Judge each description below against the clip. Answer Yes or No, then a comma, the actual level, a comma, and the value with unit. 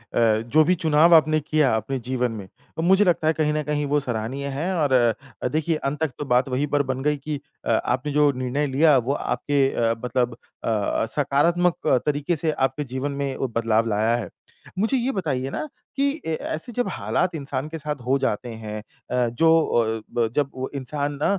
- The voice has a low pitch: No, medium, 145 Hz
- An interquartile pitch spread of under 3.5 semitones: No, average, 3.8 semitones